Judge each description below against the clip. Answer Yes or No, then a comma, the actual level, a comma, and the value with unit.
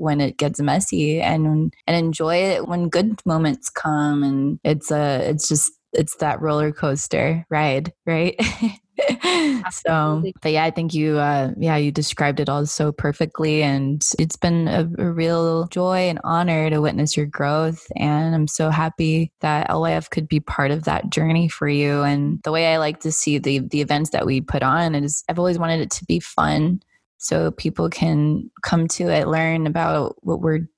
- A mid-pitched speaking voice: Yes, medium, 155 Hz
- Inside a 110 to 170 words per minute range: No, average, 185 wpm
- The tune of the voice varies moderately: No, narrow, 2.1 semitones